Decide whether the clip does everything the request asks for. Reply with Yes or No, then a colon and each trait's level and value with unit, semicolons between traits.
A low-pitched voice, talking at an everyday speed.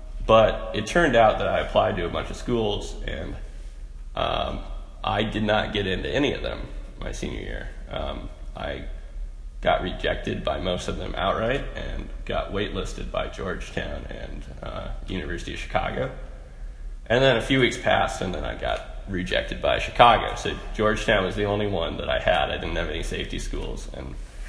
Yes: very low, 85 Hz; average, 180 wpm